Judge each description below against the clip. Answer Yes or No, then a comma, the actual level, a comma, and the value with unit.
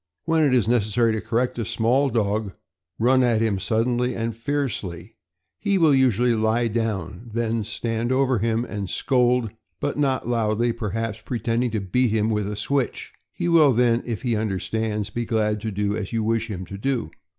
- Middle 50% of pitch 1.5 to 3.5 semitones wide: Yes, narrow, 2.5 semitones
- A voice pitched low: Yes, low, 115 Hz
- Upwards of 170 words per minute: Yes, average, 185 wpm